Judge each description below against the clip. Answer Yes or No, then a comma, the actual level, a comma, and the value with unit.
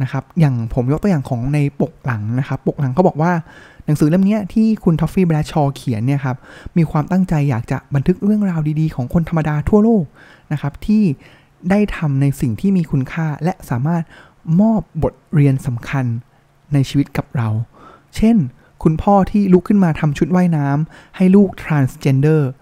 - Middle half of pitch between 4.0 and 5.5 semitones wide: Yes, average, 4.8 semitones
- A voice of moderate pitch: Yes, medium, 155 Hz